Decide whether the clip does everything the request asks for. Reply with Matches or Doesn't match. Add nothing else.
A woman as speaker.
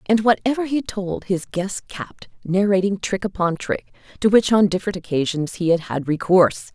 Matches